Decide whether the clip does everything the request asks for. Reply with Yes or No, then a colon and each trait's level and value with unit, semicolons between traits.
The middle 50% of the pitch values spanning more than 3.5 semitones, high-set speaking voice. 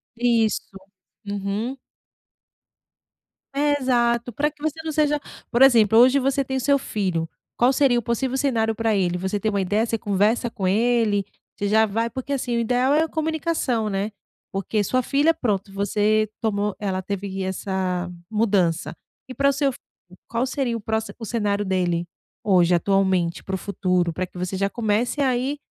Yes: average, 4.6 semitones; high, 220 Hz